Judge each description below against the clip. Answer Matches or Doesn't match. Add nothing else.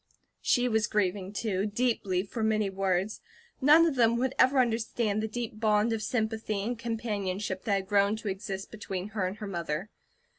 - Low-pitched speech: Doesn't match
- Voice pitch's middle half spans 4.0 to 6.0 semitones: Doesn't match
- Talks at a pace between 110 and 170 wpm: Doesn't match